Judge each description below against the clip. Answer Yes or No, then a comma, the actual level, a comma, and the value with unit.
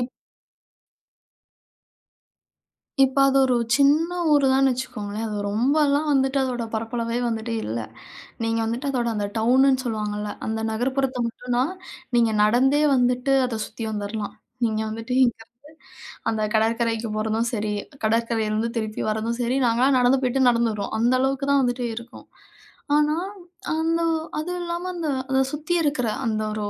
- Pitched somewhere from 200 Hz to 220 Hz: No, high, 245 Hz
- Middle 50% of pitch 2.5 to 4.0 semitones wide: Yes, average, 3.3 semitones